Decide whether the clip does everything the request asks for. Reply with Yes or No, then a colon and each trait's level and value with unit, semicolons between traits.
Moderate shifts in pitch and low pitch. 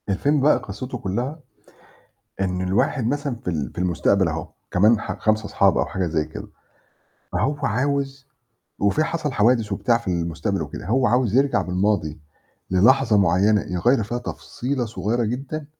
No: wide, 6.1 semitones; low, 110 Hz